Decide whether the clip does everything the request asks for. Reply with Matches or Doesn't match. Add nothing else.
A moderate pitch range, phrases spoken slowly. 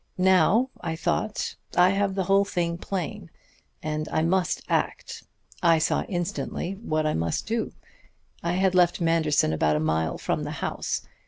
Doesn't match